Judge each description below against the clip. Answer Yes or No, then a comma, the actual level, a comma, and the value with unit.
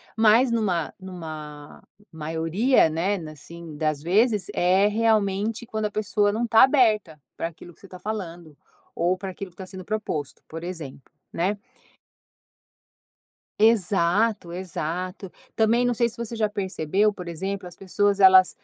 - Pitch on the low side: No, high, 190 Hz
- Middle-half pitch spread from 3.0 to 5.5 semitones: Yes, average, 4.1 semitones